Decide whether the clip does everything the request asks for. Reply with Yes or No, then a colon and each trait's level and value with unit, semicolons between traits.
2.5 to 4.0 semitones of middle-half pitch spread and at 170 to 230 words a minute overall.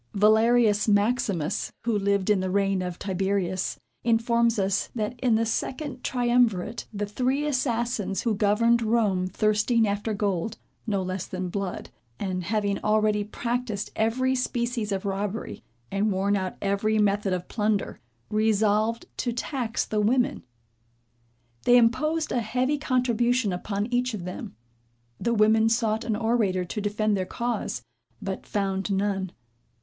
No: average, 3.1 semitones; average, 140 wpm